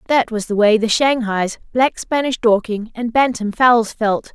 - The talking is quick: No, average, 180 wpm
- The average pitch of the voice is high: Yes, high, 230 Hz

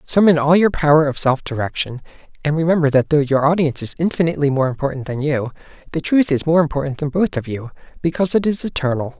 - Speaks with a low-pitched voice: No, medium, 150 Hz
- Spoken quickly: Yes, fast, 210 wpm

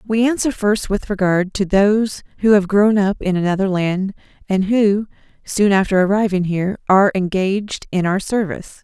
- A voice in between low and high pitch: No, high, 200 Hz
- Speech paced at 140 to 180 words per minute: Yes, average, 170 wpm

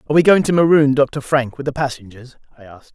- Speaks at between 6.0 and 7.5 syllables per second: Yes, 6.5 syllables/s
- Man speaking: Yes, male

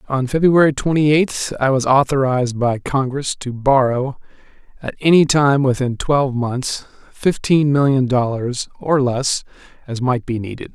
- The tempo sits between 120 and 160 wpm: Yes, average, 145 wpm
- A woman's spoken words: No, male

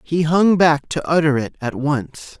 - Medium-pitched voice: Yes, medium, 155 Hz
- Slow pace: No, average, 200 wpm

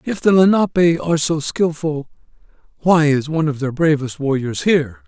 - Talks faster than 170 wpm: No, average, 165 wpm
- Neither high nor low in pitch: Yes, medium, 150 Hz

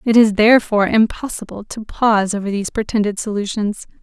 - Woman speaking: Yes, female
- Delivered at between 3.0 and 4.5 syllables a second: No, 6.1 syllables/s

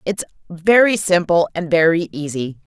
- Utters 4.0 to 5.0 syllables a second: Yes, 4.6 syllables/s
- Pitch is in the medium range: Yes, medium, 175 Hz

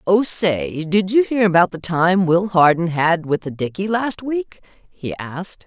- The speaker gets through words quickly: No, average, 190 wpm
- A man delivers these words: No, female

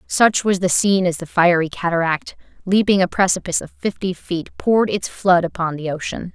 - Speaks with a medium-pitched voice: Yes, medium, 180 Hz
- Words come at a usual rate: Yes, average, 190 wpm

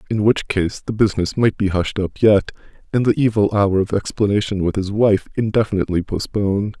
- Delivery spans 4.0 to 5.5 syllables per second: No, 5.7 syllables/s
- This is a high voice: No, low, 100 Hz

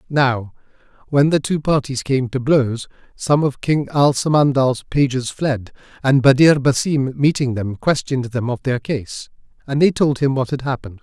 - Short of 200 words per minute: Yes, average, 175 wpm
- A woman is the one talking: No, male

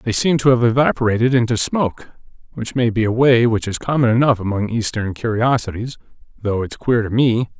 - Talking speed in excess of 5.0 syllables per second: Yes, 5.7 syllables/s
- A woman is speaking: No, male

